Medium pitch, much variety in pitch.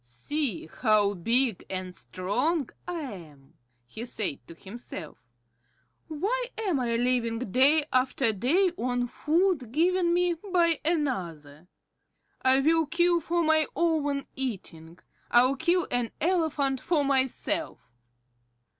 No: very high, 265 Hz; wide, 7.3 semitones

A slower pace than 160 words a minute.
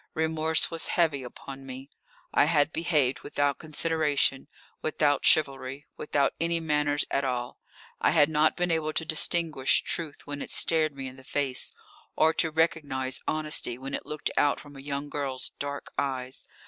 No: average, 165 wpm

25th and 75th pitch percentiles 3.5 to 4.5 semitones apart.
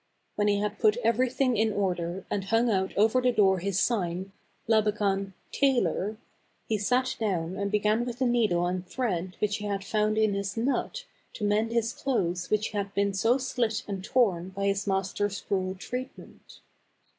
No: average, 2.9 semitones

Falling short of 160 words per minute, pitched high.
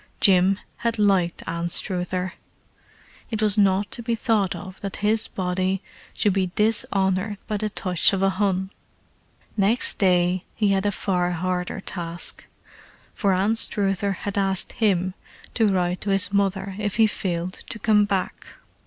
Yes: average, 150 wpm; high, 195 Hz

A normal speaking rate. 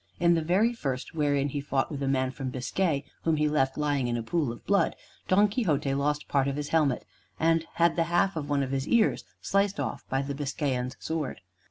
No: fast, 220 wpm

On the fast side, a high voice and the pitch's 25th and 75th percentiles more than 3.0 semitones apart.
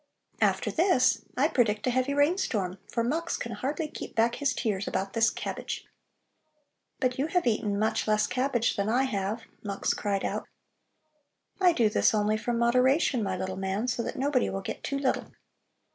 No: average, 175 wpm; high, 235 Hz; average, 4.5 semitones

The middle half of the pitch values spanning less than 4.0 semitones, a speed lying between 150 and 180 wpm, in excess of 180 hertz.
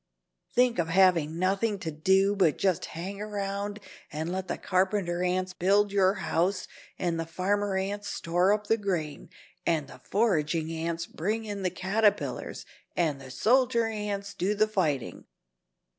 Yes: average, 3.4 semitones; average, 155 wpm; high, 190 Hz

